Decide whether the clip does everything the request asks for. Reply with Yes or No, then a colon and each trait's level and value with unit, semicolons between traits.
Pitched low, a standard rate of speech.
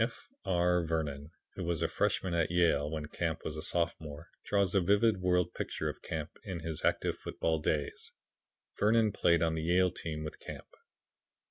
Yes: very low, 85 Hz; average, 175 wpm